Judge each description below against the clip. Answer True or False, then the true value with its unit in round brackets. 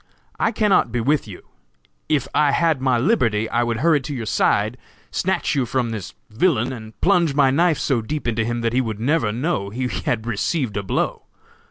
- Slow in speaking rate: False (200 wpm)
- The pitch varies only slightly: False (5.1 semitones)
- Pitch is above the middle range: False (125 Hz)